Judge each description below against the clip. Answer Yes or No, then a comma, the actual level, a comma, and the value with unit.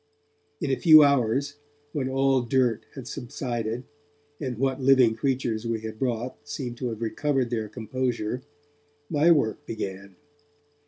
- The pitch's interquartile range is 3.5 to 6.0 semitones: No, average, 3.1 semitones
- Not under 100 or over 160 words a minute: Yes, average, 140 wpm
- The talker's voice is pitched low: Yes, low, 125 Hz